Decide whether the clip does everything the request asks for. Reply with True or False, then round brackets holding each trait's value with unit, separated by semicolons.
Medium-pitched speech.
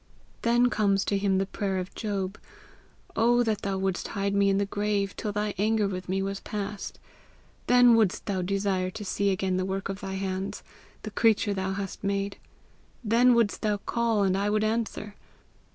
False (200 Hz)